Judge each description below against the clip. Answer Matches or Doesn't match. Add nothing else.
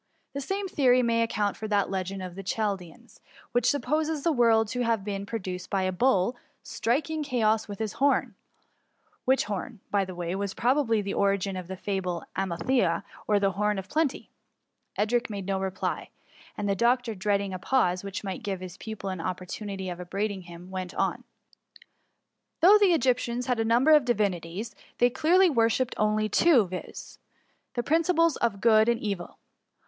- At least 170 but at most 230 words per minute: Matches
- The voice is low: Doesn't match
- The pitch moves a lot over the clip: Doesn't match